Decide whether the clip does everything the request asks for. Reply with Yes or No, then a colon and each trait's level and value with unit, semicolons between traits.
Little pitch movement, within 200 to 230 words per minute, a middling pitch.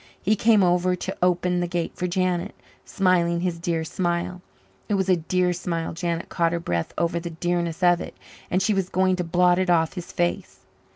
Yes: narrow, 1.2 semitones; fast, 205 wpm; medium, 175 Hz